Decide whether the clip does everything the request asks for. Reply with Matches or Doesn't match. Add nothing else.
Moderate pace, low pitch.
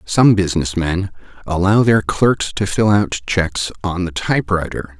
Matches